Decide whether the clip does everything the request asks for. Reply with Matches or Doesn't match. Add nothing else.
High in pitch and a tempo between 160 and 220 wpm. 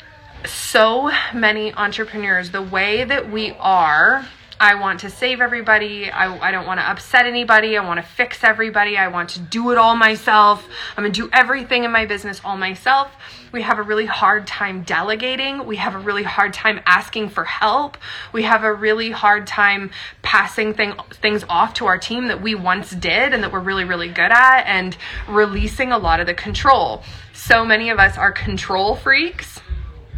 Matches